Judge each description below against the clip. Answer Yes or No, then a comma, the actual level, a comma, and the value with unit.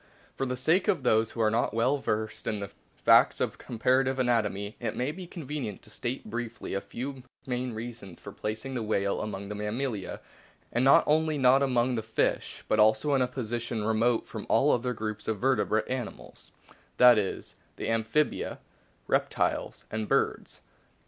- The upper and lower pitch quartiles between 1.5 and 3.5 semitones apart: Yes, average, 3.1 semitones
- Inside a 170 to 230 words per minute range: Yes, average, 180 wpm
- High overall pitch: No, low, 120 Hz